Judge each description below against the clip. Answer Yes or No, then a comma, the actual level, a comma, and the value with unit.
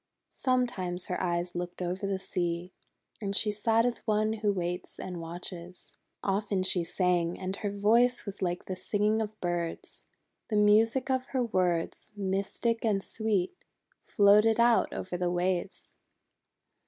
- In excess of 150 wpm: No, average, 145 wpm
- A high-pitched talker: Yes, high, 195 Hz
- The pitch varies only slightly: No, average, 3.4 semitones